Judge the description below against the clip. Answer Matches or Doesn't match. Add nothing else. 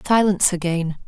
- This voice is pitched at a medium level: Matches